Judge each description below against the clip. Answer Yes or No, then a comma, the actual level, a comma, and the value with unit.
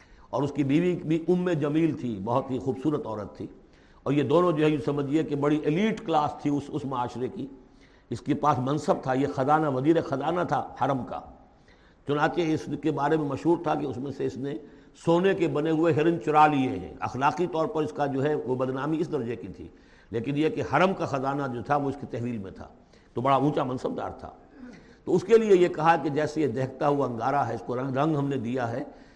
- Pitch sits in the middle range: Yes, medium, 145 Hz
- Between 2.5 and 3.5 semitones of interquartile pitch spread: Yes, average, 2.9 semitones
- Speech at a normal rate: No, fast, 240 wpm